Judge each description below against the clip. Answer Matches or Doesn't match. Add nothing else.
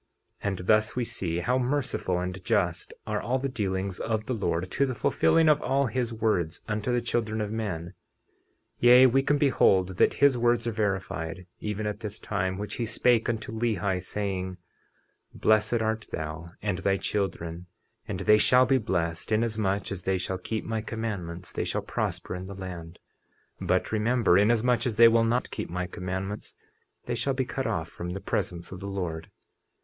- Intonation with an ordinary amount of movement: Matches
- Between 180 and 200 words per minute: Matches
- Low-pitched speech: Matches